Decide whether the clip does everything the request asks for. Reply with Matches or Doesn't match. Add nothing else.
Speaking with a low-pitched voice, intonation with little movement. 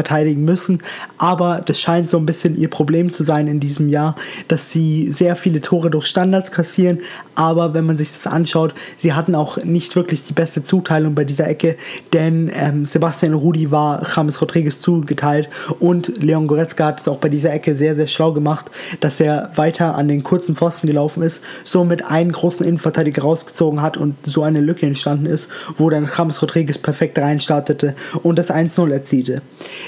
Doesn't match